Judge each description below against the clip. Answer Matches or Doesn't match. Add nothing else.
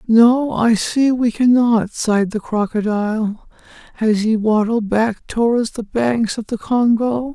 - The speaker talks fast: Doesn't match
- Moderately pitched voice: Doesn't match